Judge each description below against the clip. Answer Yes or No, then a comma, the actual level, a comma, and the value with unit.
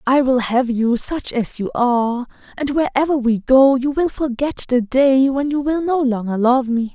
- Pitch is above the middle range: Yes, very high, 260 Hz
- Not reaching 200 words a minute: No, fast, 205 wpm